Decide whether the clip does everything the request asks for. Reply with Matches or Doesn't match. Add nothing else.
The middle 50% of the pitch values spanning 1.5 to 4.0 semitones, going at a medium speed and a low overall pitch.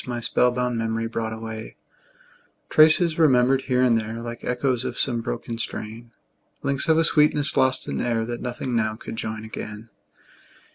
Matches